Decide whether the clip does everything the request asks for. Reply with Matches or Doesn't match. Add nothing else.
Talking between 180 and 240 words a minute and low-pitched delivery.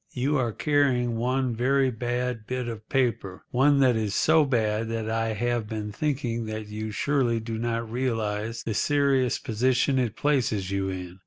Doesn't match